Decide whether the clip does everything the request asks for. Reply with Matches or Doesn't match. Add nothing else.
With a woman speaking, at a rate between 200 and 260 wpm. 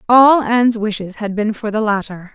Matches